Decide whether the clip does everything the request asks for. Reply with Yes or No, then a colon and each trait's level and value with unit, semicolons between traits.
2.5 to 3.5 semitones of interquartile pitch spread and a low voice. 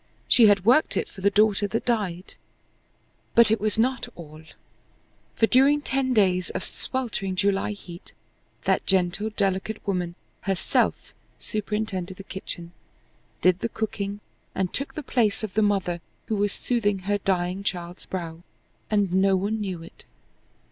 No: average, 2.9 semitones; high, 200 Hz